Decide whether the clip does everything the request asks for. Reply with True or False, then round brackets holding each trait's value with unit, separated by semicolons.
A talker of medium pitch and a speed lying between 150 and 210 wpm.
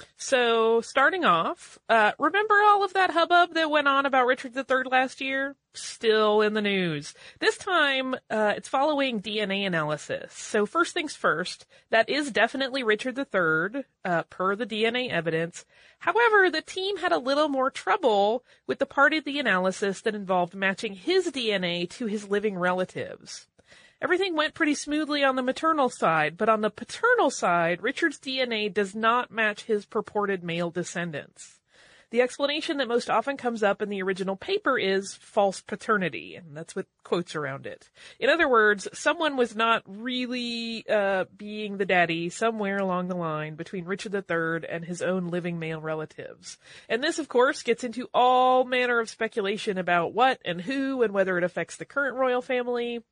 False (225 Hz; 175 wpm)